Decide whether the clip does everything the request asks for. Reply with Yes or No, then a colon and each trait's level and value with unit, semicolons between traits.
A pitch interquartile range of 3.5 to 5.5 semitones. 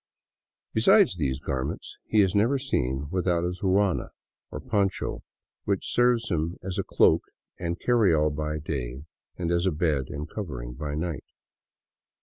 Yes: average, 5.2 semitones